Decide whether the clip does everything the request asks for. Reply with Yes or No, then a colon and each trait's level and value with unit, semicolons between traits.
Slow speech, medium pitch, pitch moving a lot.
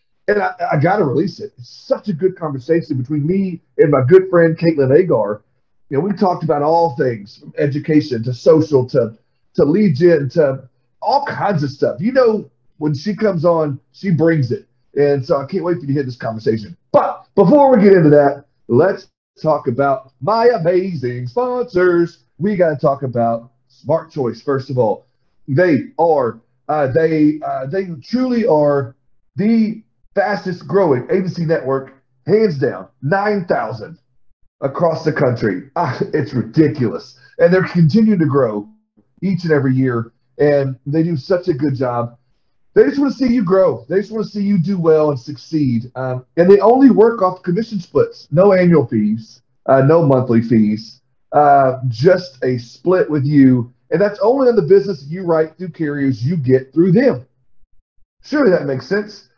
No: average, 175 wpm; medium, 155 Hz; wide, 6.3 semitones